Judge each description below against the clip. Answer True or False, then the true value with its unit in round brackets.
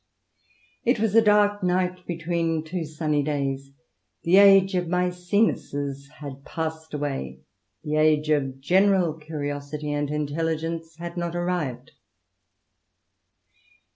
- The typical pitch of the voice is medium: True (160 Hz)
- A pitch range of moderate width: True (3.5 semitones)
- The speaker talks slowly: True (115 wpm)